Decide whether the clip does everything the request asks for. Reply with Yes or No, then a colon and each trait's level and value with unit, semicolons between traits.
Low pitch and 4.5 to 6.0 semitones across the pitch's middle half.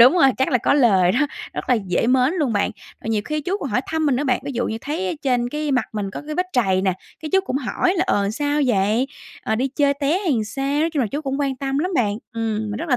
No: very high, 265 Hz; average, 5.1 semitones